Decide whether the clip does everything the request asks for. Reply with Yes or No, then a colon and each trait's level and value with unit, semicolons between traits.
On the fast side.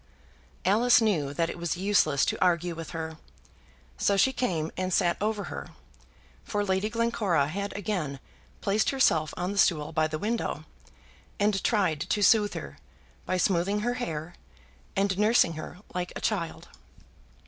No: average, 155 wpm